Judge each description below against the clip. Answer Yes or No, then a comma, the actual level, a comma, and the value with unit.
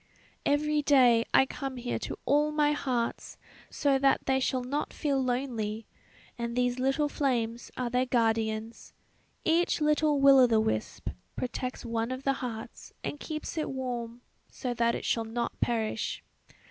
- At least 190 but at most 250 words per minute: No, average, 160 wpm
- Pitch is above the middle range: Yes, very high, 255 Hz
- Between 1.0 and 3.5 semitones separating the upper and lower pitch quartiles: Yes, average, 3.1 semitones